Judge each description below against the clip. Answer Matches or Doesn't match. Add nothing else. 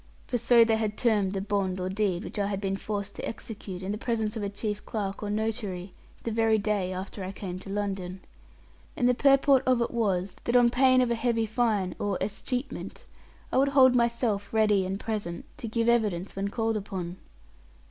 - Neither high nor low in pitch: Doesn't match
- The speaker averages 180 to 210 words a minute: Matches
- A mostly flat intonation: Doesn't match